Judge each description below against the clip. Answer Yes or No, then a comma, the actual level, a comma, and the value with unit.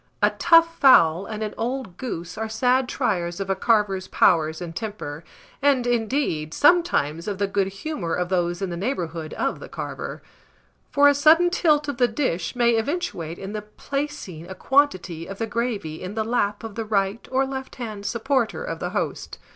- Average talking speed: Yes, average, 185 wpm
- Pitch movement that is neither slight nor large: No, wide, 6.6 semitones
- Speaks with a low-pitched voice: No, high, 215 Hz